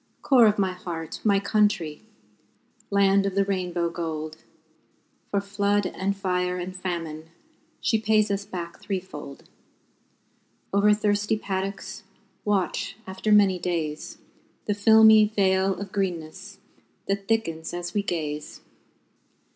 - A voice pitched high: Yes, high, 195 Hz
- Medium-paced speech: No, slow, 120 wpm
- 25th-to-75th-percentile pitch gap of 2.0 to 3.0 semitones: Yes, average, 2.7 semitones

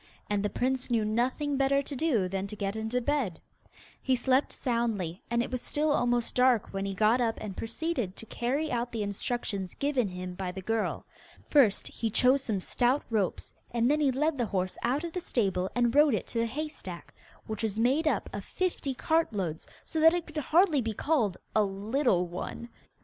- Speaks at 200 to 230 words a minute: Yes, fast, 205 wpm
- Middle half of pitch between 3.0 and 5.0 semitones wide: No, wide, 5.4 semitones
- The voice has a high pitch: Yes, high, 235 Hz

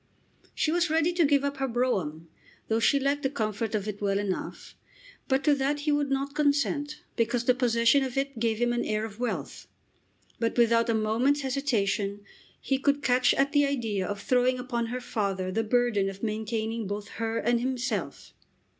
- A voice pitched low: No, high, 240 Hz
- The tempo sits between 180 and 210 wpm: Yes, average, 190 wpm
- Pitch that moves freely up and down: No, average, 4.1 semitones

